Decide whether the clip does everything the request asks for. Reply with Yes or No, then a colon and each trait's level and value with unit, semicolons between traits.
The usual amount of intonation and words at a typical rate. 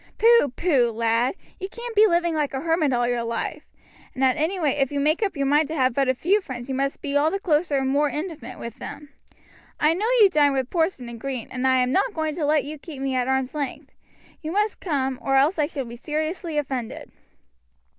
No: average, 3.7 semitones; fast, 235 wpm